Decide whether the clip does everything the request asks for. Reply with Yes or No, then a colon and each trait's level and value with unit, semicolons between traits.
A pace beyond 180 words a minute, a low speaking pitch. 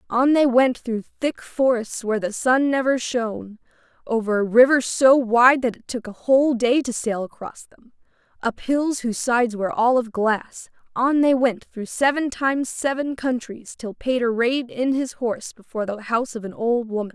No: average, 190 wpm; high, 240 Hz